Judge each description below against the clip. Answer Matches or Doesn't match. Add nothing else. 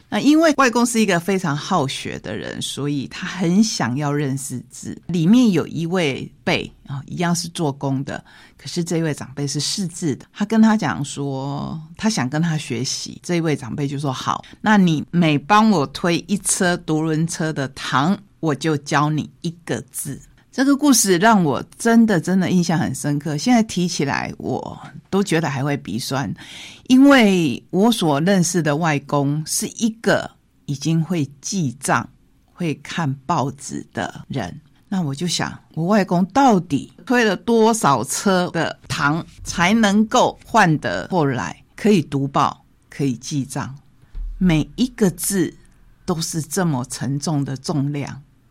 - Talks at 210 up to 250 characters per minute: Matches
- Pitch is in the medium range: Matches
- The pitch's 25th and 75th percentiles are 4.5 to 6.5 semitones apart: Matches